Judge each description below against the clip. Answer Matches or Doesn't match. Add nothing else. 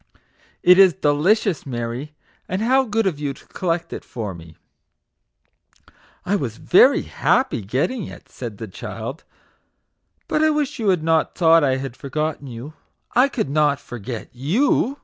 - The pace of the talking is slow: Doesn't match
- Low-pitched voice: Doesn't match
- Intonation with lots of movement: Matches